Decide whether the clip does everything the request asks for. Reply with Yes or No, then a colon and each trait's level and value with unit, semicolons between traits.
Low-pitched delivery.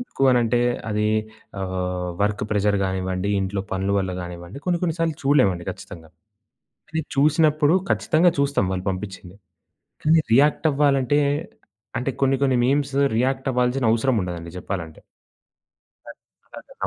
Yes: low, 115 Hz